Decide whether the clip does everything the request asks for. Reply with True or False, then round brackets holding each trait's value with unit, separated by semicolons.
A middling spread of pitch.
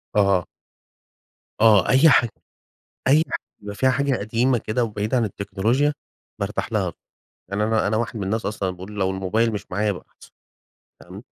True (3.0 semitones)